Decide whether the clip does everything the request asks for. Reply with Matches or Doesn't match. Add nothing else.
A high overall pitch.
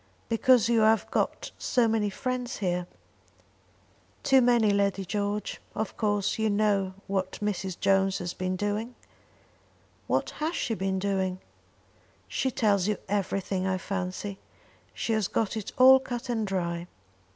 Matches